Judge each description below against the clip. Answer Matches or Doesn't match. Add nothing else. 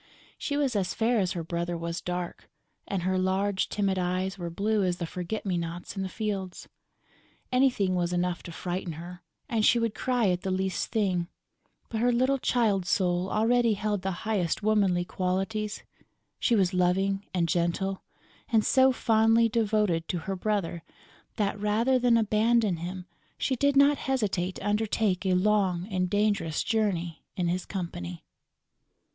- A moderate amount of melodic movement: Matches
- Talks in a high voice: Matches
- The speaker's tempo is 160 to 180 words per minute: Matches